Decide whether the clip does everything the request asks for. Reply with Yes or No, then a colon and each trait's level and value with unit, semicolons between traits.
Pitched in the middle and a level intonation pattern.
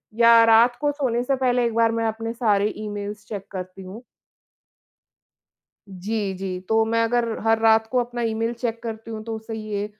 No: high, 225 Hz; narrow, 1.7 semitones